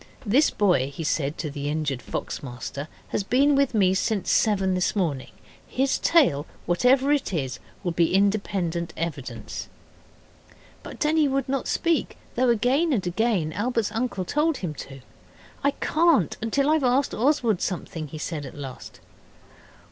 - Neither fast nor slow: Yes, average, 155 wpm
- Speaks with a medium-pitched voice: No, high, 200 Hz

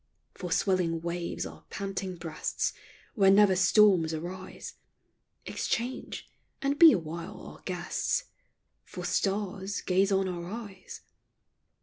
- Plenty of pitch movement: No, narrow, 2.6 semitones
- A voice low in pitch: No, high, 190 Hz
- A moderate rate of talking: No, slow, 110 wpm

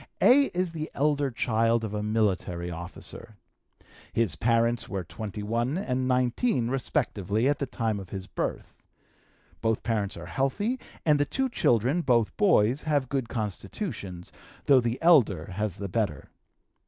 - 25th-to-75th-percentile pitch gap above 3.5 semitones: Yes, average, 5.3 semitones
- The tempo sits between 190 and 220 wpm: No, average, 145 wpm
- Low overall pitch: Yes, low, 115 Hz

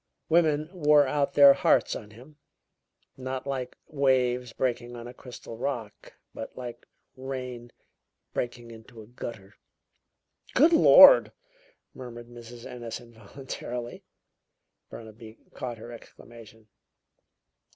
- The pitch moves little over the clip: Yes, narrow, 2.2 semitones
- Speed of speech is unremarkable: No, slow, 110 wpm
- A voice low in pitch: Yes, low, 120 Hz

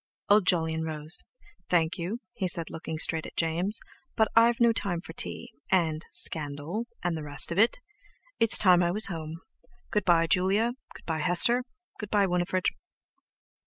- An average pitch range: Yes, average, 4.3 semitones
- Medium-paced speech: Yes, average, 165 wpm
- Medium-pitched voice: Yes, medium, 175 Hz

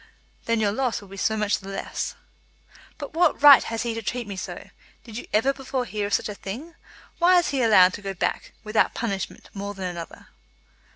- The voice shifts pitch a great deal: No, average, 4.5 semitones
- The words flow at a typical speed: No, fast, 225 wpm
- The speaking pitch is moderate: No, high, 220 Hz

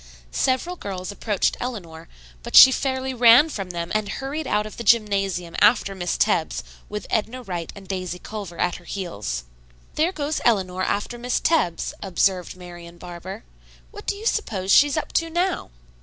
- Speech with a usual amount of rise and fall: No, wide, 6.3 semitones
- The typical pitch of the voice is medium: No, high, 205 Hz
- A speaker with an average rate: Yes, average, 170 wpm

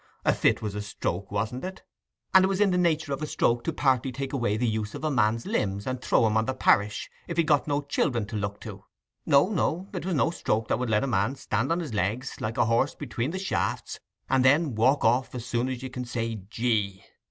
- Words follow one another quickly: Yes, fast, 250 wpm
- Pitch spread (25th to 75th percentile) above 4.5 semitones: Yes, average, 4.9 semitones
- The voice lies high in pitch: No, low, 125 Hz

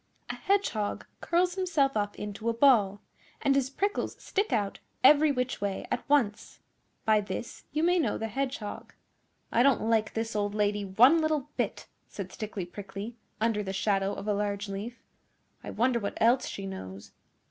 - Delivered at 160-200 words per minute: Yes, average, 170 wpm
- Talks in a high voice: Yes, high, 225 Hz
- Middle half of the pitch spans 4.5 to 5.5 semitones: Yes, average, 5.1 semitones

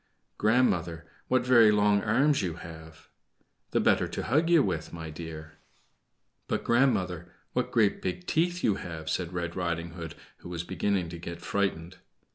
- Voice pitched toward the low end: Yes, very low, 90 Hz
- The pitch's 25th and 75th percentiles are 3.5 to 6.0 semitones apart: Yes, average, 5.2 semitones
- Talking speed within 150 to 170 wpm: Yes, average, 160 wpm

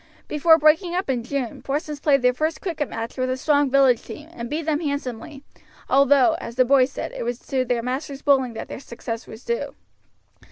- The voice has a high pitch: Yes, very high, 275 Hz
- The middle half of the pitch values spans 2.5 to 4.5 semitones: Yes, average, 3.2 semitones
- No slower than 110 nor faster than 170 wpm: No, fast, 205 wpm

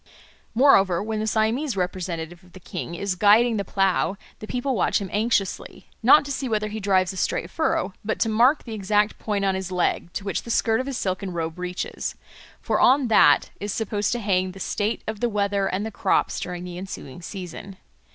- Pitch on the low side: No, high, 200 Hz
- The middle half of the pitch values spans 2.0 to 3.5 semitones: Yes, average, 3.1 semitones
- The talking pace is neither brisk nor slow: No, fast, 210 wpm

